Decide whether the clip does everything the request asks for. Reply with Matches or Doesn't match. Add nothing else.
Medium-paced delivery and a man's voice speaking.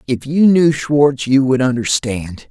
Matches